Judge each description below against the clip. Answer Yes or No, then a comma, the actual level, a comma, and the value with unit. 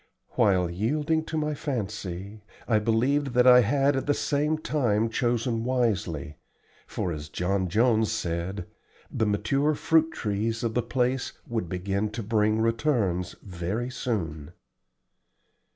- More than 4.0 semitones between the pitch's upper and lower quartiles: Yes, average, 4.9 semitones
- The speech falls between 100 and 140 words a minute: Yes, slow, 135 wpm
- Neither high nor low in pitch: No, low, 115 Hz